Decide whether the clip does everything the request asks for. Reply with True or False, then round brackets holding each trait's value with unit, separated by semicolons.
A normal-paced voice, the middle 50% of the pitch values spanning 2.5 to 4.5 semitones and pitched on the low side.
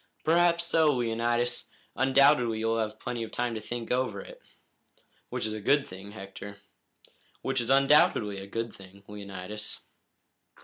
True (145 wpm; 4.2 semitones; 115 Hz)